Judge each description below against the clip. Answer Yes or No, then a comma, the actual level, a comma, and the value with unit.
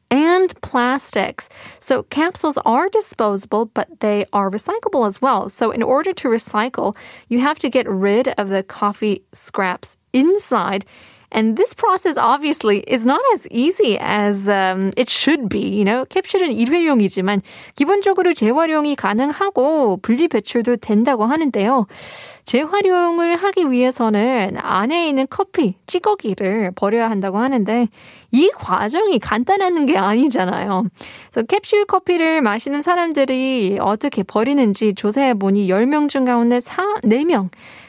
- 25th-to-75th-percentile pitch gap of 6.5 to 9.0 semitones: Yes, wide, 7.7 semitones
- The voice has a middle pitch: No, very high, 255 Hz